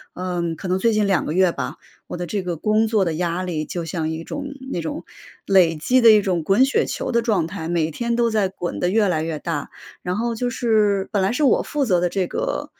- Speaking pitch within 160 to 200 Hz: Yes, high, 190 Hz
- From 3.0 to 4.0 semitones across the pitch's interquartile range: No, average, 4.5 semitones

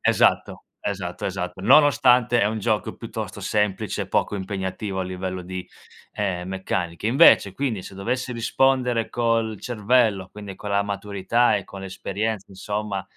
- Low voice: Yes, low, 105 Hz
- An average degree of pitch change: Yes, average, 3.3 semitones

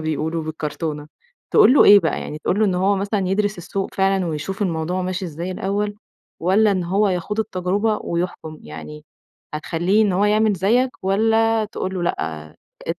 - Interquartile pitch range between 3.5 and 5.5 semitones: Yes, average, 4.0 semitones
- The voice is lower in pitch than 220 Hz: Yes, medium, 185 Hz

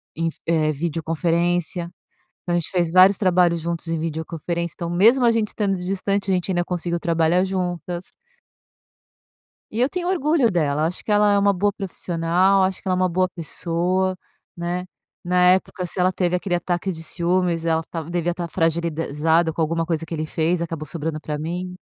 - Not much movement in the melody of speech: Yes, narrow, 2.1 semitones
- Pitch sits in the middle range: Yes, medium, 175 Hz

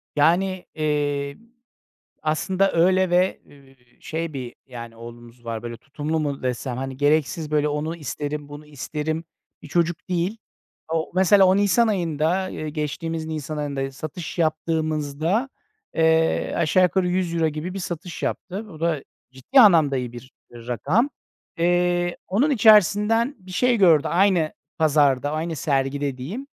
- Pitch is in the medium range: Yes, medium, 160 Hz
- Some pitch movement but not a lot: Yes, average, 3.9 semitones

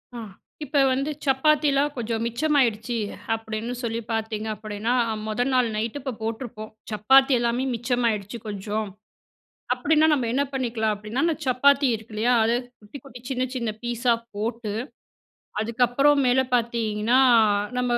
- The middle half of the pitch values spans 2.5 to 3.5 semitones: Yes, average, 3.2 semitones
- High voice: Yes, high, 235 Hz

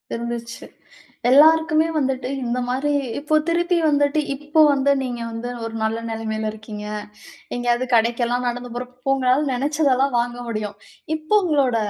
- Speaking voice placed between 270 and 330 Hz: No, very high, 250 Hz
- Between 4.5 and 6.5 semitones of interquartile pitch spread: No, average, 3.7 semitones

